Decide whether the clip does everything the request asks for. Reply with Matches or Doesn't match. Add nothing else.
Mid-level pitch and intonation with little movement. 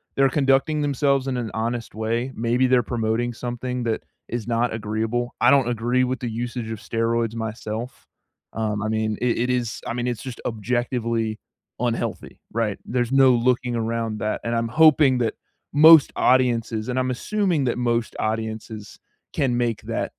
Doesn't match